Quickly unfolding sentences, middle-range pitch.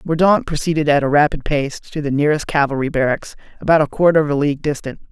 Yes: fast, 210 wpm; medium, 145 Hz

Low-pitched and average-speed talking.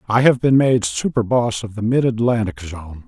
Yes: low, 115 Hz; average, 195 wpm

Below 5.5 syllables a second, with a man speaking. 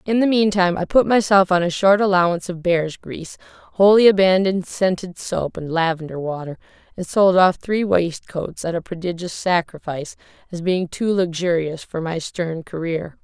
No: 5.1 syllables/s; female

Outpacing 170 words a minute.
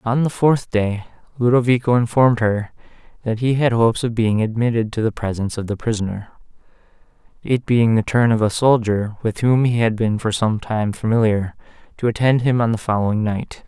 Yes: average, 190 wpm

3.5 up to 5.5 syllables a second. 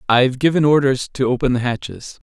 No: 5.9 syllables/s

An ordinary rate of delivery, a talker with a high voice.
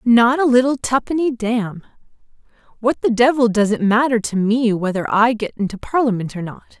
Yes: average, 175 wpm; high, 230 Hz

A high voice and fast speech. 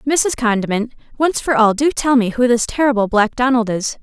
Yes: high, 240 Hz; fast, 210 wpm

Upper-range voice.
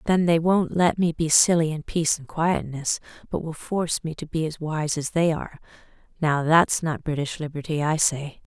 No: medium, 160 Hz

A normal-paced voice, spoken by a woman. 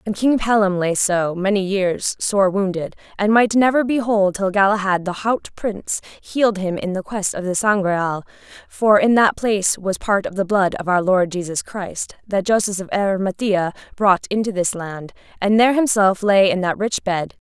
Yes: average, 195 wpm; female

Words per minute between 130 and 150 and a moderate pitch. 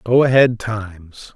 No: slow, 135 wpm; low, 110 Hz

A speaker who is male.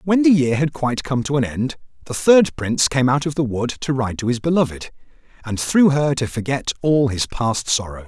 Yes: male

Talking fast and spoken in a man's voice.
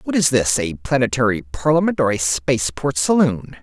No: average, 165 wpm; male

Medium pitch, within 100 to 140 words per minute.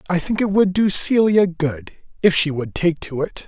No: medium, 175 Hz; fast, 205 wpm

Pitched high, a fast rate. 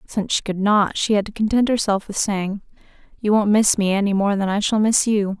Yes: high, 205 Hz; fast, 245 wpm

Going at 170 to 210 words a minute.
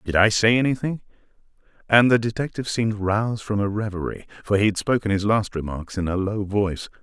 Yes: average, 195 wpm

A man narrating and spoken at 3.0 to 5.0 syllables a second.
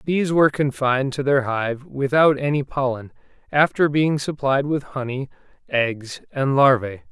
Yes: male; 4.5 syllables/s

